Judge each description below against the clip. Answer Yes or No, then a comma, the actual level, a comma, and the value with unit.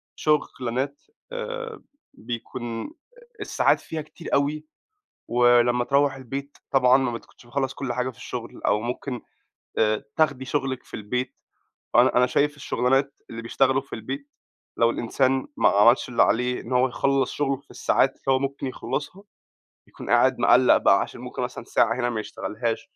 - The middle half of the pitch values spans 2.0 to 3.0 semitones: Yes, narrow, 2.5 semitones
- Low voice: Yes, low, 130 Hz